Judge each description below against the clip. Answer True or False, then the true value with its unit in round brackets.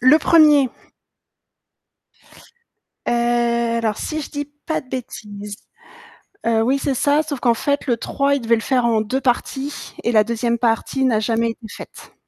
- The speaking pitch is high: True (240 Hz)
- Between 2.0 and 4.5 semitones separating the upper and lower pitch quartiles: True (3.3 semitones)